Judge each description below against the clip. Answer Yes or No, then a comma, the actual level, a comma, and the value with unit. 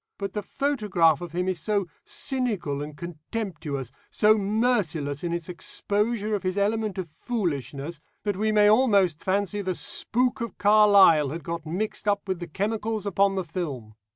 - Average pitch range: Yes, average, 4.1 semitones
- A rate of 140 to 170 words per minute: Yes, average, 165 wpm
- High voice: Yes, high, 195 Hz